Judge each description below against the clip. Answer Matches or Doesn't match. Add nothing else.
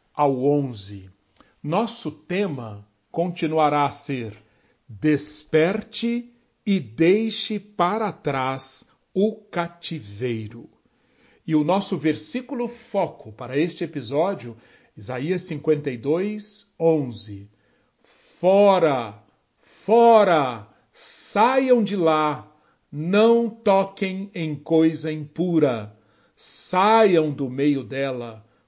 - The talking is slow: Matches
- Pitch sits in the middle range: Matches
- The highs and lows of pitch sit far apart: Matches